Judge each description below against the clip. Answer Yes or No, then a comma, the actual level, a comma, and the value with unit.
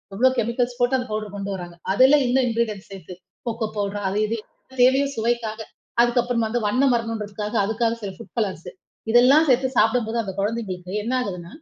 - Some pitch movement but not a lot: Yes, average, 3.1 semitones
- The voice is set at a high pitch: Yes, high, 225 Hz